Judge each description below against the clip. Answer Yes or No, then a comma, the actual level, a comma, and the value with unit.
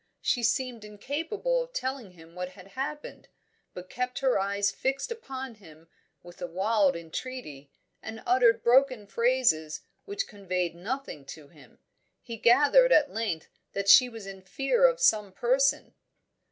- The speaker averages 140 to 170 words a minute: Yes, average, 150 wpm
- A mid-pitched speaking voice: No, high, 230 Hz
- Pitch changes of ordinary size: No, wide, 6.3 semitones